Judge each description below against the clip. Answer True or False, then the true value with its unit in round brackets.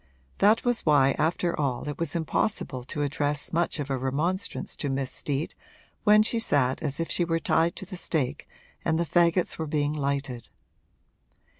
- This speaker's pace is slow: False (175 wpm)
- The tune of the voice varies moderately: True (3.6 semitones)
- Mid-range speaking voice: True (155 Hz)